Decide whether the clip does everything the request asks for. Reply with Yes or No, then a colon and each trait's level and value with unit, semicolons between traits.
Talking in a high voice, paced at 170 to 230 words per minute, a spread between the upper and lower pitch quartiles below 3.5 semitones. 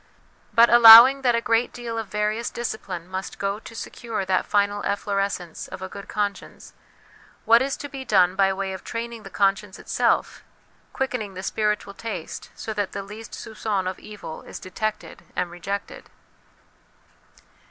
No: high, 210 Hz; average, 160 wpm; average, 2.8 semitones